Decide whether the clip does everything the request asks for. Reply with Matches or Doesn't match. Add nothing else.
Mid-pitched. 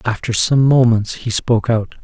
Doesn't match